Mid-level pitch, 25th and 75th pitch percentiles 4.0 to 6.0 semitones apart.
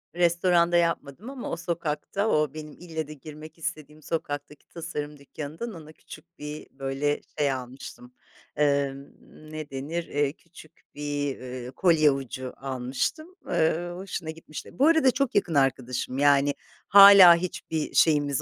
No: medium, 150 Hz; average, 3.3 semitones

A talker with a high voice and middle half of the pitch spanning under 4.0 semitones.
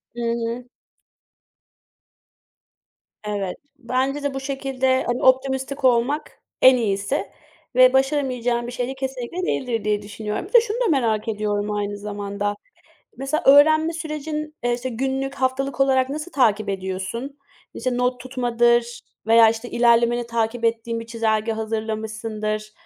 Yes: high, 240 Hz; average, 3.4 semitones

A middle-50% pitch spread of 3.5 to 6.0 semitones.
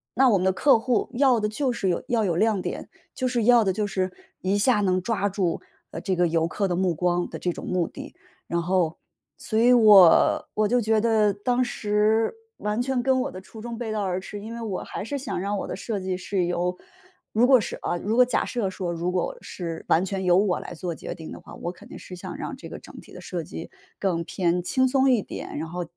Yes: average, 4.3 semitones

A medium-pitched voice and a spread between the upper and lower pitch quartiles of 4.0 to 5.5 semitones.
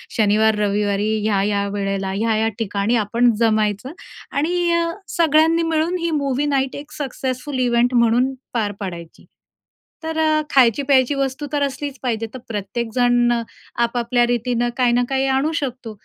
No: high, 245 Hz; average, 4.4 semitones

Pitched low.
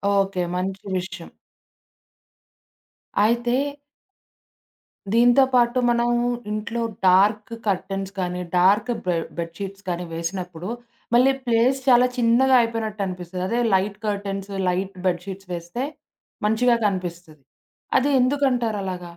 No: high, 200 Hz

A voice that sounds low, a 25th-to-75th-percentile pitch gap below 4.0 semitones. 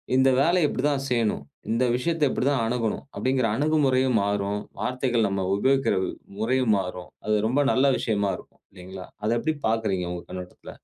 No: low, 120 Hz; average, 4.5 semitones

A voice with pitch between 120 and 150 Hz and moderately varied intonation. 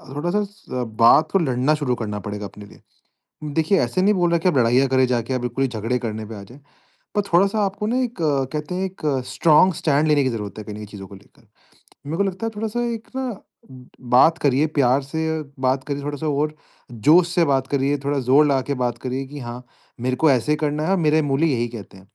Yes: medium, 140 Hz; average, 4.8 semitones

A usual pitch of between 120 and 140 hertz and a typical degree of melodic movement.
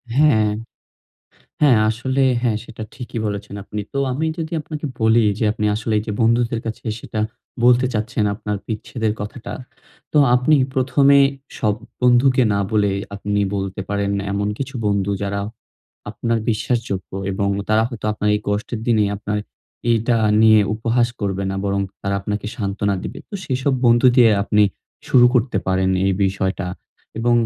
No: low, 110 Hz; average, 3.2 semitones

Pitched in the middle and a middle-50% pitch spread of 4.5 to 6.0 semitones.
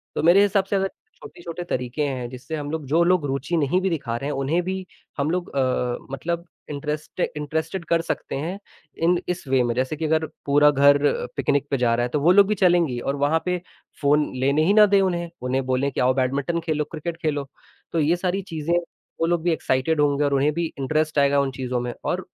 No: medium, 150 Hz; average, 3.9 semitones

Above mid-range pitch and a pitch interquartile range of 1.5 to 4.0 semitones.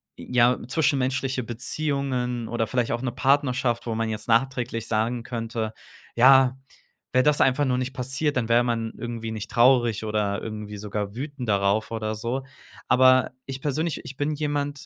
No: low, 125 Hz; average, 2.8 semitones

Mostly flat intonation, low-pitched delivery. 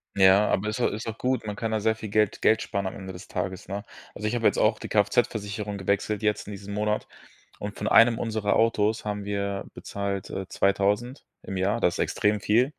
Yes: narrow, 1.7 semitones; low, 105 Hz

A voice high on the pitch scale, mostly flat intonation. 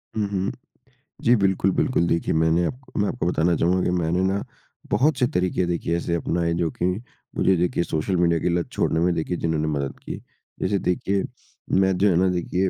No: very low, 90 Hz; narrow, 2.3 semitones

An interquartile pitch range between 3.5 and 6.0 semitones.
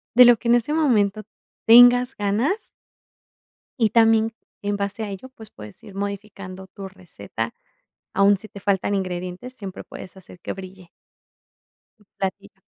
No: average, 2.9 semitones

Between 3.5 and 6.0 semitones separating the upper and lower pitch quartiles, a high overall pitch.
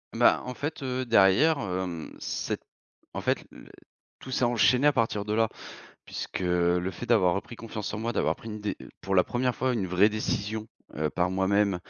No: average, 4.4 semitones; low, 105 Hz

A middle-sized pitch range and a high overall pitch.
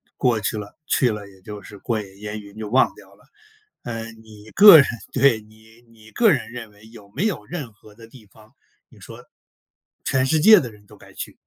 No: average, 3.1 semitones; low, 110 Hz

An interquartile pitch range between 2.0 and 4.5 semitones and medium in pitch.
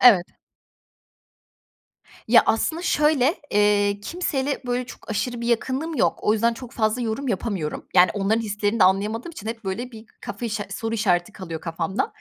No: average, 3.4 semitones; high, 220 Hz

